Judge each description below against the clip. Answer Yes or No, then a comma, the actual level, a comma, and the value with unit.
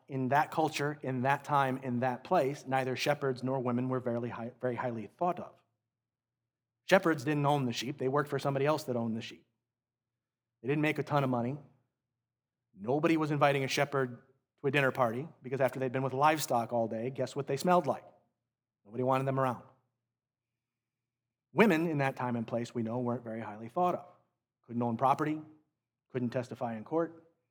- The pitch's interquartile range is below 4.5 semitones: Yes, average, 2.9 semitones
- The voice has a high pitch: No, low, 130 Hz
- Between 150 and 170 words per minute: No, average, 185 wpm